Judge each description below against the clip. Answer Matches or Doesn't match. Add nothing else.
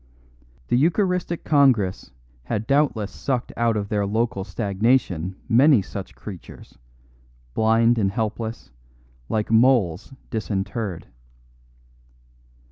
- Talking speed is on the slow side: Matches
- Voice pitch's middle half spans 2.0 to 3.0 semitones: Doesn't match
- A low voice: Matches